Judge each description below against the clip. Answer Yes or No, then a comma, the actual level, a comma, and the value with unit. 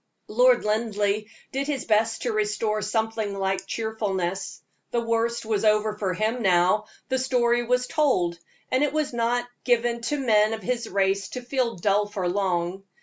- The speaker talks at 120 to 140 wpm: No, average, 165 wpm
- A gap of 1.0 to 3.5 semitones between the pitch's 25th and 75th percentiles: Yes, average, 3.2 semitones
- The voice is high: Yes, high, 220 Hz